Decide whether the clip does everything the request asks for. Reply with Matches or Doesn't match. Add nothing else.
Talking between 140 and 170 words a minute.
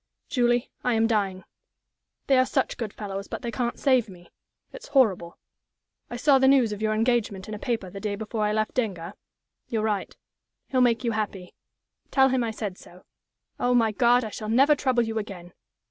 Doesn't match